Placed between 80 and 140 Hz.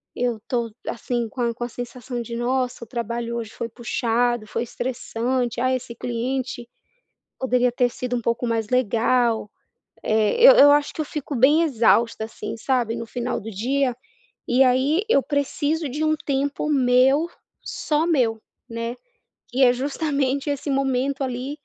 No: very high, 250 Hz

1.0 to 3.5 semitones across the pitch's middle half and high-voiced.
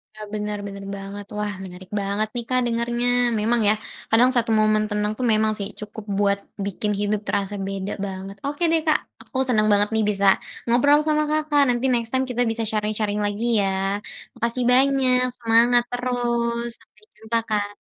Yes: average, 2.9 semitones; high, 220 Hz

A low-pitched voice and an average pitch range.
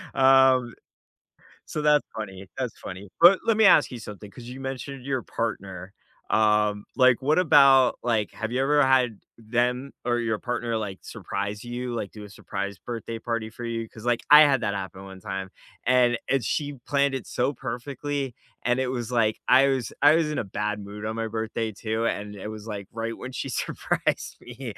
Yes: low, 120 Hz; average, 3.8 semitones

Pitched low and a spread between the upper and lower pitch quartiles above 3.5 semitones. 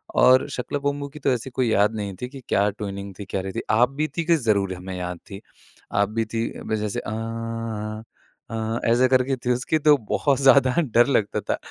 Yes: low, 115 Hz; average, 4.1 semitones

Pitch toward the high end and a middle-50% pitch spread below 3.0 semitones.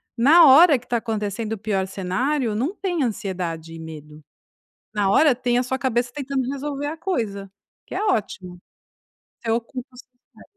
No: high, 235 Hz; wide, 5.6 semitones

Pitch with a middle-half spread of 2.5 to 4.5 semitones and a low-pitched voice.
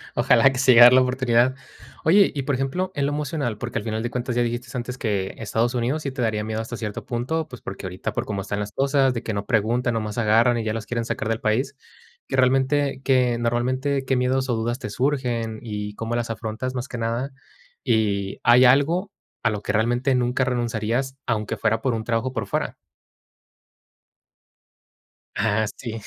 Yes: average, 2.8 semitones; low, 120 Hz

